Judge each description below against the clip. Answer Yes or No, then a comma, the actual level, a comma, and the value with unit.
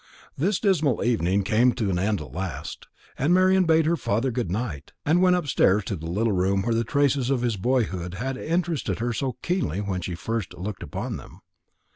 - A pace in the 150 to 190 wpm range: No, average, 200 wpm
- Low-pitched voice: Yes, low, 115 Hz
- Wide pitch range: Yes, wide, 7.0 semitones